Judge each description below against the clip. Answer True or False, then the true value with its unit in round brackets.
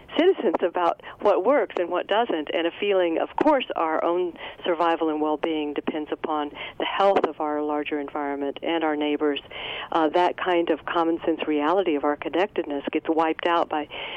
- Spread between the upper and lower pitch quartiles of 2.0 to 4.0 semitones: True (2.7 semitones)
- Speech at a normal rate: True (180 wpm)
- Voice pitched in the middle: True (160 Hz)